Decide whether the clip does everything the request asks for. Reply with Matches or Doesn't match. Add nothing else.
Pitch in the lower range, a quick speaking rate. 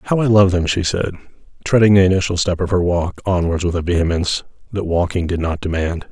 Matches